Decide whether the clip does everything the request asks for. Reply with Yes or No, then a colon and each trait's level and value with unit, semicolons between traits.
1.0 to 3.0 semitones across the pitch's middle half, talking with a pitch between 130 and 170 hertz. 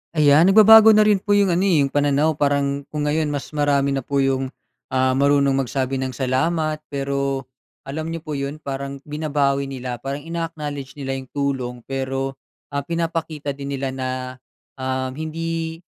Yes: narrow, 2.6 semitones; medium, 140 Hz